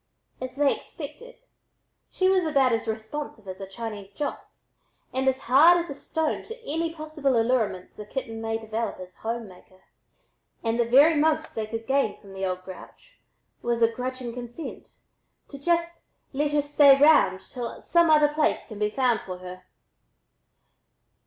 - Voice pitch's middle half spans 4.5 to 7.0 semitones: Yes, average, 5.3 semitones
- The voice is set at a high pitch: Yes, very high, 250 Hz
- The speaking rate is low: No, average, 170 wpm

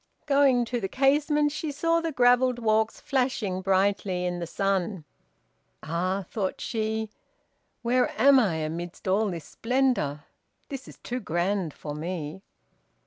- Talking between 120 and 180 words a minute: Yes, average, 140 wpm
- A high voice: Yes, high, 215 Hz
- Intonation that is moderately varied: No, wide, 6.2 semitones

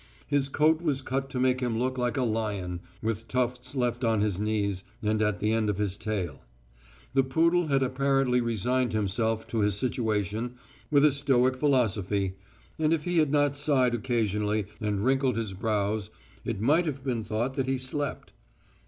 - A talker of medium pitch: No, low, 125 Hz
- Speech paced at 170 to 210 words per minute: Yes, average, 180 wpm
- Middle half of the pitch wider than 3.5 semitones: Yes, average, 4.0 semitones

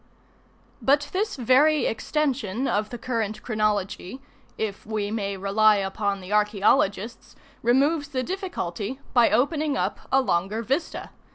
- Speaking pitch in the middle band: No, high, 225 Hz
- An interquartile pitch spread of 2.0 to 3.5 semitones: No, average, 5.1 semitones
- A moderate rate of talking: No, slow, 125 wpm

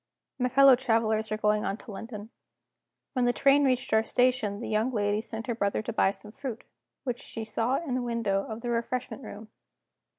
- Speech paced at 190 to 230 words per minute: Yes, average, 200 wpm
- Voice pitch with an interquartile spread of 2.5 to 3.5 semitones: Yes, average, 2.8 semitones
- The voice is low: No, high, 230 Hz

